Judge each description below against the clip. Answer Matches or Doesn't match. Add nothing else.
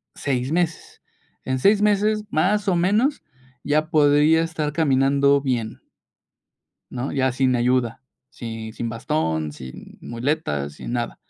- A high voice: Doesn't match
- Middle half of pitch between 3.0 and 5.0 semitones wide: Doesn't match